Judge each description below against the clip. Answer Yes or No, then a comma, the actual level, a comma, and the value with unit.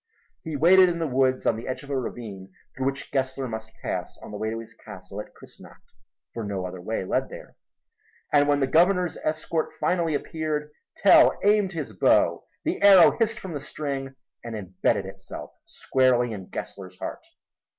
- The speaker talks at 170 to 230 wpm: Yes, average, 180 wpm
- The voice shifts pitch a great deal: Yes, wide, 6.3 semitones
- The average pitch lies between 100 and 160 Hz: Yes, low, 135 Hz